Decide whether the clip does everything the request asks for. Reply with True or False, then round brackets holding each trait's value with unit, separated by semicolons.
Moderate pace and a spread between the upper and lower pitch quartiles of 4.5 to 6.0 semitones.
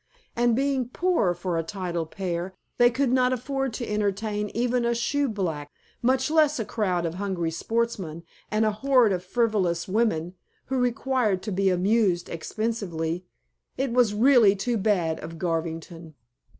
True (150 wpm; 5.5 semitones)